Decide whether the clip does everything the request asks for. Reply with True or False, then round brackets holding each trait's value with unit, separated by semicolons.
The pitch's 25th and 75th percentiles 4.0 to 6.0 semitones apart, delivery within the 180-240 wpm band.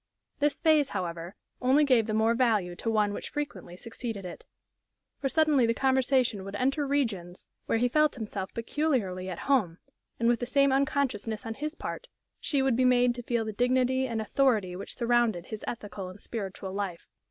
True (4.7 semitones; 185 wpm)